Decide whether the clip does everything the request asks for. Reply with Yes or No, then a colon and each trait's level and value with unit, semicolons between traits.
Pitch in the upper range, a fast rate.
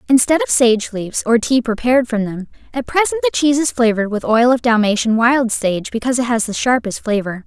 Yes: high, 240 Hz; fast, 215 wpm